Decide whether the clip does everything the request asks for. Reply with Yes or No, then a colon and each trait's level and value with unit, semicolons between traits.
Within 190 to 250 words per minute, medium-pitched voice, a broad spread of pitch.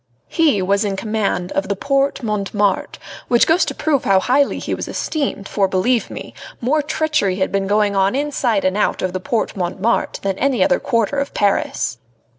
No: average, 195 wpm; high, 210 Hz; wide, 5.9 semitones